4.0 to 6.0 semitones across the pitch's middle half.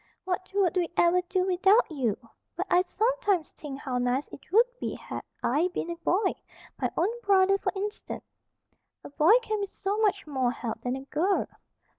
Yes: average, 5.0 semitones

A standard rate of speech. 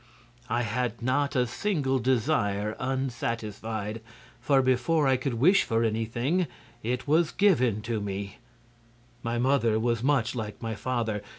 No: slow, 130 wpm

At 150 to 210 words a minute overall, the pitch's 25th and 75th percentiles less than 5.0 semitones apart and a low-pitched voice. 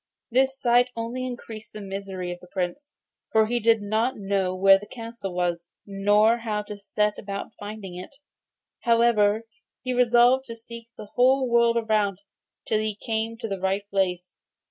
No: average, 165 wpm; average, 3.1 semitones; high, 215 Hz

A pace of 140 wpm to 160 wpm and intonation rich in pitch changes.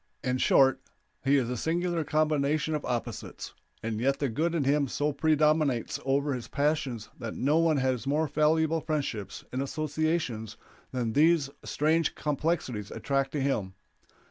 No: average, 150 wpm; average, 3.3 semitones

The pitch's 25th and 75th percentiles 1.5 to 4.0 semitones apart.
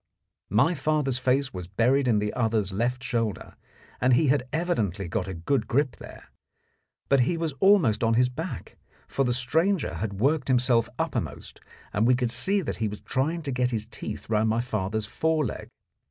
No: average, 4.5 semitones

